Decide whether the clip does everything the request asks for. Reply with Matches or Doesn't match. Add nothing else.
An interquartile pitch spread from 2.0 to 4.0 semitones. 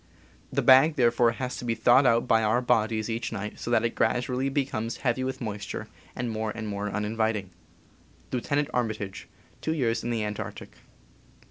Matches